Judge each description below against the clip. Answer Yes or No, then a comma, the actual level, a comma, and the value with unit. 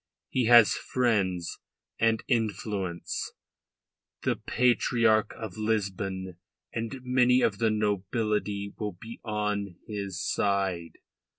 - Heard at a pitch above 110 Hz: No, low, 105 Hz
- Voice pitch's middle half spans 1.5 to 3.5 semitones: Yes, average, 2.7 semitones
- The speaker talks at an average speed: No, slow, 100 wpm